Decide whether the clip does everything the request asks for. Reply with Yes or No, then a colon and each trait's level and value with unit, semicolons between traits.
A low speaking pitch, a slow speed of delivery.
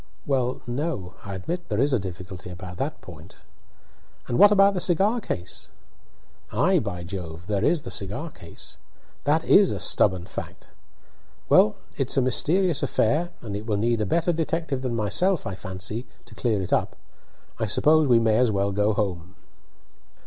No: low, 115 Hz; average, 170 wpm